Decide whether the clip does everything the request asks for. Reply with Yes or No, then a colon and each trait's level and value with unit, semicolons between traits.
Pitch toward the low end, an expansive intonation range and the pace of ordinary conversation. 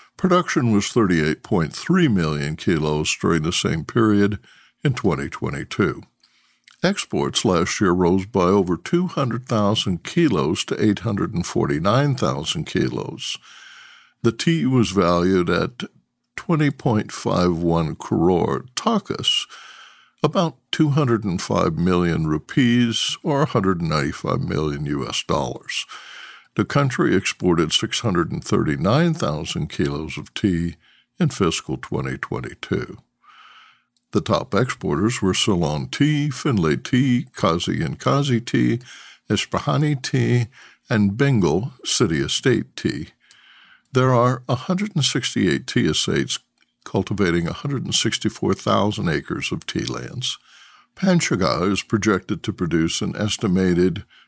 No: low, 110 Hz; wide, 8.3 semitones; slow, 110 wpm